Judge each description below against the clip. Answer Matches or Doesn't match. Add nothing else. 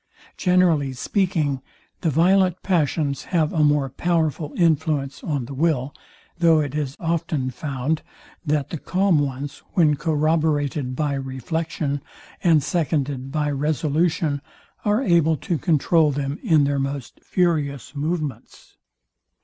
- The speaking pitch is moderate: Matches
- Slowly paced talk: Matches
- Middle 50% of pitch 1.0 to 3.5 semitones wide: Matches